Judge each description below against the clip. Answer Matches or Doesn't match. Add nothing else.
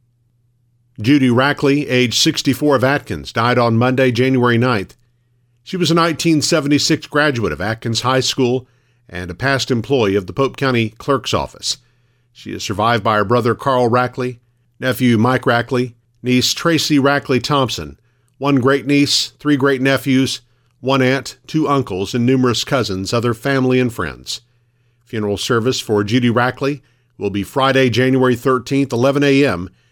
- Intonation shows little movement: Matches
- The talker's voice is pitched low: Matches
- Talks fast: Doesn't match